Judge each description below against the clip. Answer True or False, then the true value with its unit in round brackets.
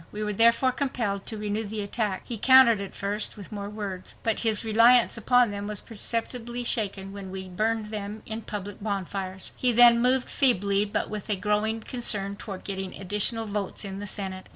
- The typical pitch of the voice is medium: False (210 Hz)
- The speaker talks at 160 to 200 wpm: True (190 wpm)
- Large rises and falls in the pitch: False (2.5 semitones)